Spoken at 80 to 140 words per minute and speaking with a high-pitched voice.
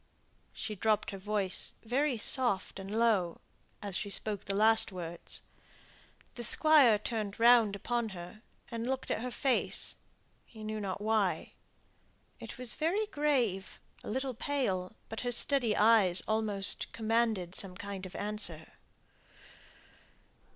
Yes: slow, 135 wpm; high, 215 Hz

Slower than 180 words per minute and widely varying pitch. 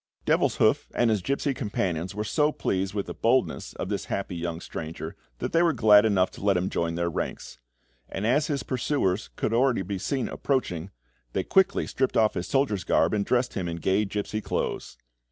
No: average, 195 wpm; wide, 5.9 semitones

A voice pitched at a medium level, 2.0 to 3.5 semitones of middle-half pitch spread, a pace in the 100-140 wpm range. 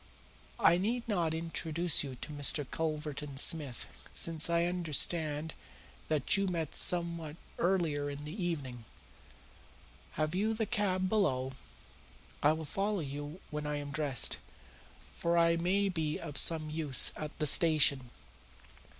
Yes: medium, 160 Hz; average, 3.0 semitones; slow, 135 wpm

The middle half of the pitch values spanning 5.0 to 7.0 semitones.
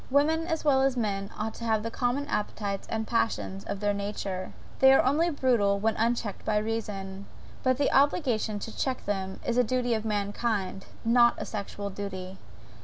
No: average, 3.9 semitones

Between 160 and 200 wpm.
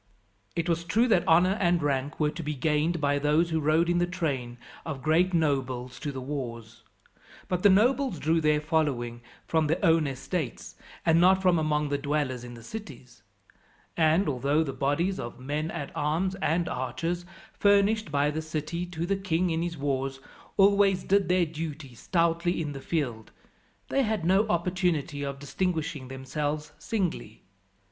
Yes: average, 170 wpm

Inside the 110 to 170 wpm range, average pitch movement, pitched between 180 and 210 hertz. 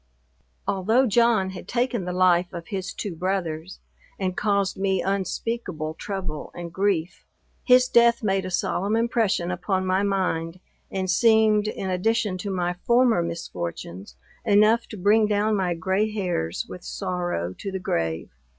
Yes: average, 150 wpm; average, 3.2 semitones; high, 190 Hz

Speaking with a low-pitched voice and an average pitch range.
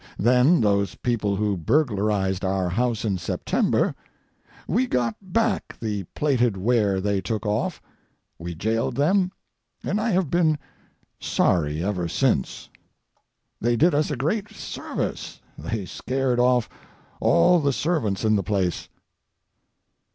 No: low, 115 Hz; wide, 6.5 semitones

